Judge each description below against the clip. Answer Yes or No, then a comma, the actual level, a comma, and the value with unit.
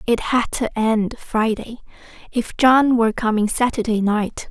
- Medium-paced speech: Yes, average, 145 wpm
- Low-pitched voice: No, high, 230 Hz